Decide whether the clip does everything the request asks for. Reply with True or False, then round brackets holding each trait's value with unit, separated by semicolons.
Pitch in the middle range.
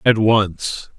False (105 Hz)